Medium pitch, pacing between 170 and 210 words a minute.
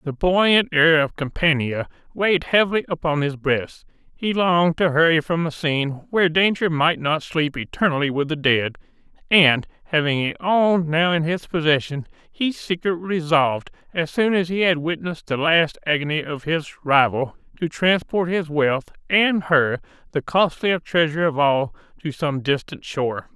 No: medium, 160 Hz; average, 160 wpm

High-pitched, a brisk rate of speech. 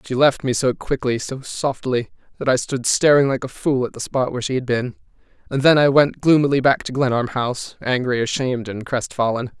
No: low, 130 Hz; fast, 215 wpm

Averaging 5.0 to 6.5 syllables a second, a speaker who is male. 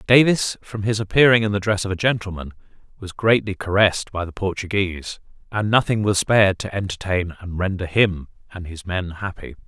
Yes: 5.6 syllables/s; male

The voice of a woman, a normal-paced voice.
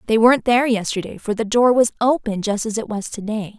No: female; fast, 250 wpm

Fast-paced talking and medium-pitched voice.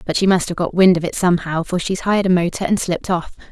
Yes: fast, 290 wpm; medium, 180 Hz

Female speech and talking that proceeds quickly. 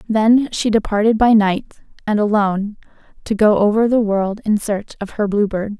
No: female; average, 185 wpm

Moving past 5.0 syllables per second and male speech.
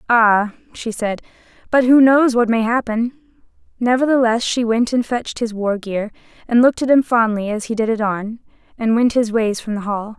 No: 5.2 syllables/s; female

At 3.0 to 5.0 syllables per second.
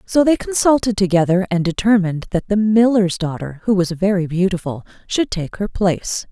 No: 5.3 syllables/s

